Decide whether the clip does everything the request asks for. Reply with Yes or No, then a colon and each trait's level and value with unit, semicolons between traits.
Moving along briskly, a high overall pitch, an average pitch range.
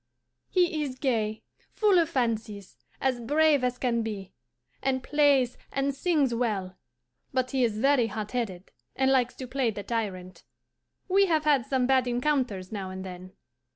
No: average, 155 wpm; very high, 250 Hz; average, 4.4 semitones